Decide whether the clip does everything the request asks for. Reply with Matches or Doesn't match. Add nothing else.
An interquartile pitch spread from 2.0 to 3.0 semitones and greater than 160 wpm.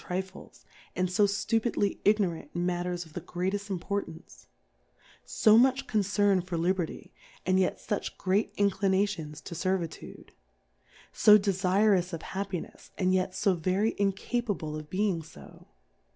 Doesn't match